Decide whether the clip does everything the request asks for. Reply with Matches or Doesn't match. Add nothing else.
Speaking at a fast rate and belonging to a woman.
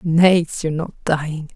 Doesn't match